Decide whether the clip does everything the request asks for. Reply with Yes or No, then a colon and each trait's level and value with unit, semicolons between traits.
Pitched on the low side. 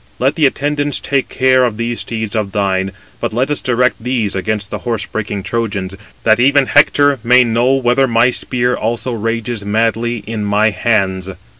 Yes: low, 115 Hz